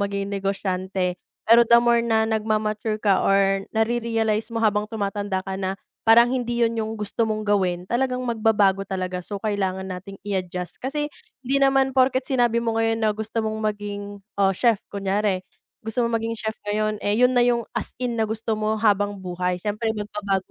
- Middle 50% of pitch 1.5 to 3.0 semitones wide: Yes, narrow, 2.6 semitones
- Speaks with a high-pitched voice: Yes, high, 215 Hz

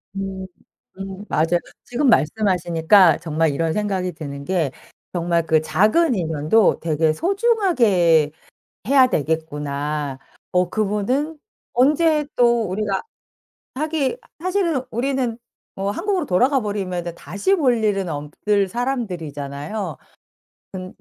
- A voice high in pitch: Yes, high, 195 Hz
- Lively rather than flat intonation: Yes, wide, 7.4 semitones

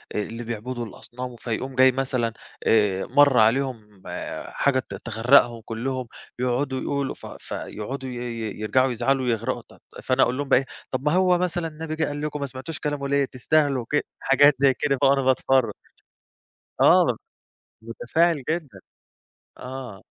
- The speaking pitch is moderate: No, low, 130 Hz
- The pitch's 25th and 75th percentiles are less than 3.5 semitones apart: Yes, average, 2.9 semitones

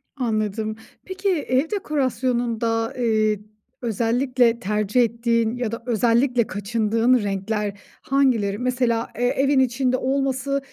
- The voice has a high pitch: Yes, high, 235 Hz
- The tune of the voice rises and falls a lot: No, average, 2.8 semitones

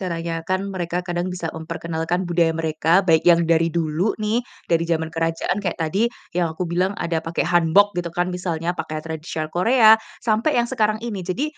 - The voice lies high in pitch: No, medium, 170 Hz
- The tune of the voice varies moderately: No, narrow, 2.3 semitones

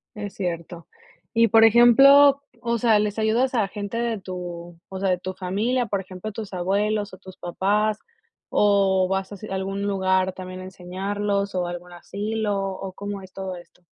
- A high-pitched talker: Yes, high, 195 Hz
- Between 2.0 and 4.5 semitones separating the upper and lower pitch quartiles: Yes, narrow, 2.5 semitones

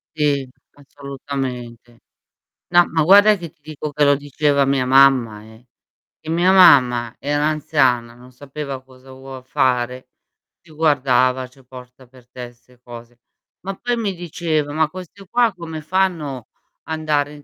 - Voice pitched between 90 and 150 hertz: Yes, medium, 140 Hz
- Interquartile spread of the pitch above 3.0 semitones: Yes, average, 3.7 semitones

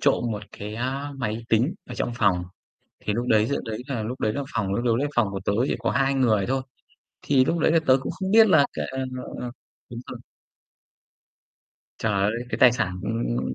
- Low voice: Yes, low, 120 Hz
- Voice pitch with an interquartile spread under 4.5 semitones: Yes, average, 4.1 semitones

